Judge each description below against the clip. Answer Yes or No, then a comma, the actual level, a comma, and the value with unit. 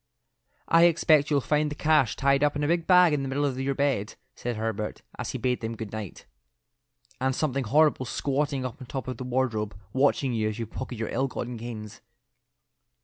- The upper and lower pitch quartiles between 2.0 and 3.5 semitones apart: No, average, 4.1 semitones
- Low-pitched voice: Yes, low, 130 Hz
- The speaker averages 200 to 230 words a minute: Yes, fast, 205 wpm